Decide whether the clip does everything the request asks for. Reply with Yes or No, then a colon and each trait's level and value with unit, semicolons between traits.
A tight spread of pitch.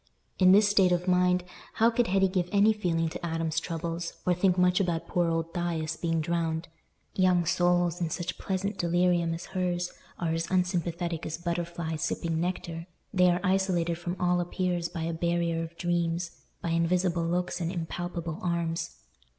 Yes: narrow, 1.4 semitones